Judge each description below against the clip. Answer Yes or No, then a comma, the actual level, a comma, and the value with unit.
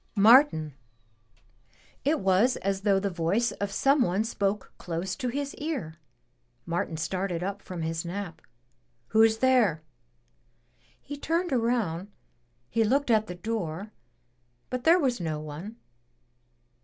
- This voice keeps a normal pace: No, slow, 130 wpm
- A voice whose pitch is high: Yes, high, 200 Hz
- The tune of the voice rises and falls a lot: Yes, wide, 6.2 semitones